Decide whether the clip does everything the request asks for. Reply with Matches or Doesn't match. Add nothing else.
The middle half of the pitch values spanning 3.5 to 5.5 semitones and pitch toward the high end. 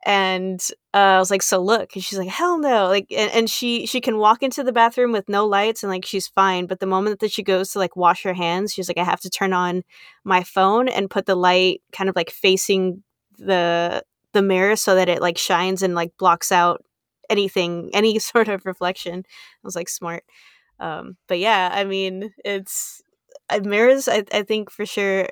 Doesn't match